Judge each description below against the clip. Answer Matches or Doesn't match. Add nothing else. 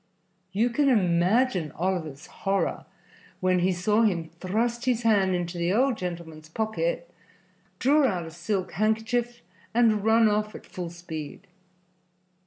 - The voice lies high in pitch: Matches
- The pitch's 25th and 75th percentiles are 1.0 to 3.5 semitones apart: Doesn't match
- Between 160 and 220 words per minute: Doesn't match